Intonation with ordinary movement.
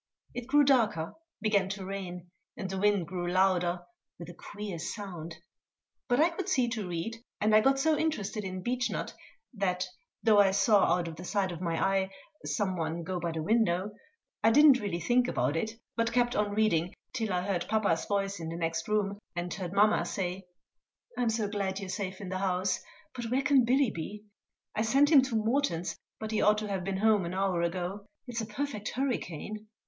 Yes: average, 3.8 semitones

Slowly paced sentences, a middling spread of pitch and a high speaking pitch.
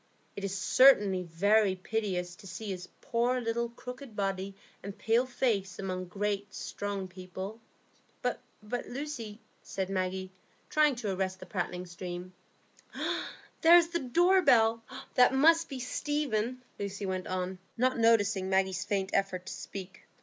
No: average, 145 wpm; average, 4.4 semitones; high, 205 Hz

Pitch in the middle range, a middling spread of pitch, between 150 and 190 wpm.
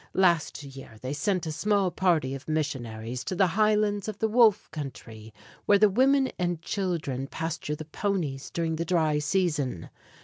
No: medium, 165 Hz; wide, 5.8 semitones; average, 165 wpm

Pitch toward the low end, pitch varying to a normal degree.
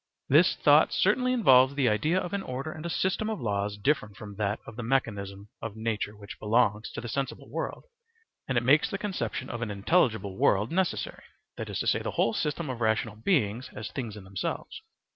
No: low, 115 Hz; wide, 6.0 semitones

